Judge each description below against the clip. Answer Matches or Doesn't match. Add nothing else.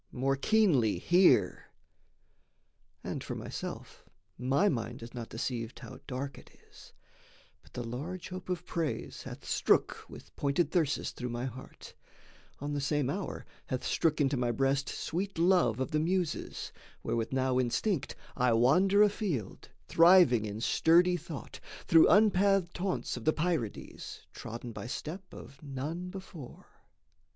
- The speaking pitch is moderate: Matches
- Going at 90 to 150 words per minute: Matches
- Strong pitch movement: Matches